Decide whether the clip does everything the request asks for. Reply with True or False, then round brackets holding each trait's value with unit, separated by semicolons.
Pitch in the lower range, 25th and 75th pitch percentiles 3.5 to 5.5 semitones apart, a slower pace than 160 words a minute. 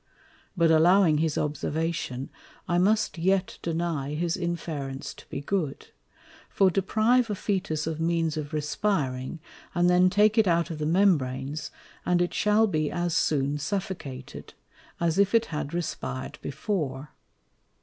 False (165 Hz; 4.0 semitones; 140 wpm)